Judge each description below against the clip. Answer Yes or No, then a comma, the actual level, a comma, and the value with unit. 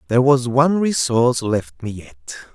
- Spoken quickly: No, average, 165 wpm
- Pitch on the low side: Yes, low, 125 Hz